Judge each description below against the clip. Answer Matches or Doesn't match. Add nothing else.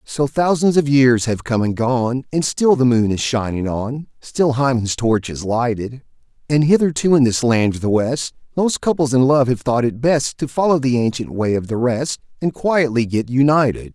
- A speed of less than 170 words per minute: Doesn't match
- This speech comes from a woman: Doesn't match